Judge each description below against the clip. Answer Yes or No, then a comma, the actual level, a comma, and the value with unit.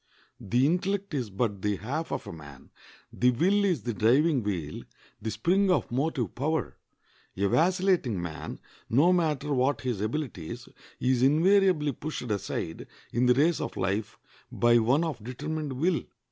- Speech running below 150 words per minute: No, average, 155 wpm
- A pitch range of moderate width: No, wide, 6.8 semitones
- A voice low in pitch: Yes, low, 130 Hz